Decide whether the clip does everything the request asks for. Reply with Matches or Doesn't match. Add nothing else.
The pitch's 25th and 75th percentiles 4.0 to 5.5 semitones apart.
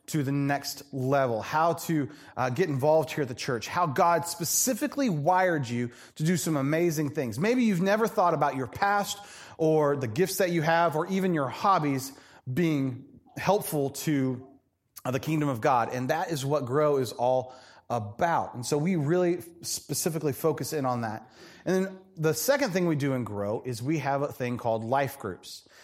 Matches